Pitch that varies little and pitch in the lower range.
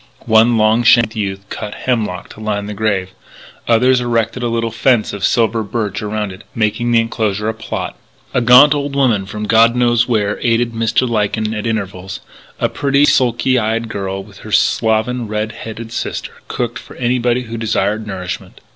Yes: narrow, 2.1 semitones; low, 110 Hz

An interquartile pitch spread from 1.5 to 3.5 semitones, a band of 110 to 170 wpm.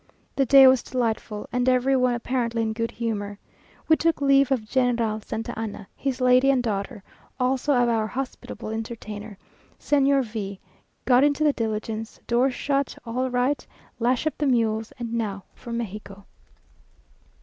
Yes: average, 3.1 semitones; average, 160 wpm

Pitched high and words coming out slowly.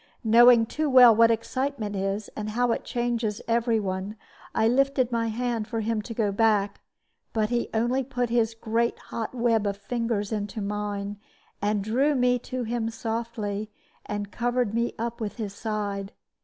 No: high, 225 Hz; average, 170 wpm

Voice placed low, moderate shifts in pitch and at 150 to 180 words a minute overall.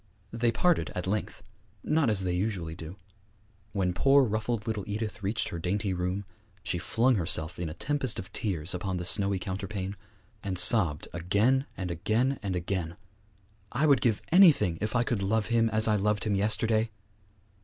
Yes: low, 105 Hz; average, 3.9 semitones; average, 175 wpm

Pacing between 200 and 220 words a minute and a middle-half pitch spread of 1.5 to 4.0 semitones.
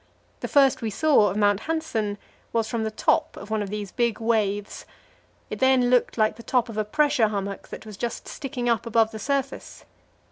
Yes: fast, 205 wpm; average, 3.3 semitones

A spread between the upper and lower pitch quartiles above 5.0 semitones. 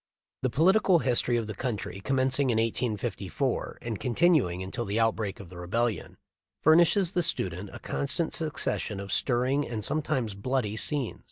Yes: wide, 5.4 semitones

